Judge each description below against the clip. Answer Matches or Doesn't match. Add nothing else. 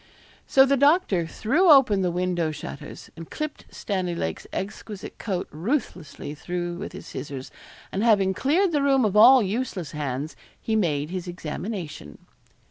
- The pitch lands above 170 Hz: Matches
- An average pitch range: Doesn't match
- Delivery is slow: Doesn't match